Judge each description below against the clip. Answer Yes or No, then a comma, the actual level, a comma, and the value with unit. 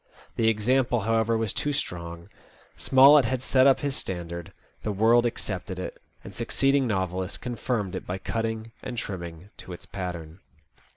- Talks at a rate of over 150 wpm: Yes, average, 160 wpm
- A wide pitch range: No, average, 5.0 semitones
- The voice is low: Yes, low, 110 Hz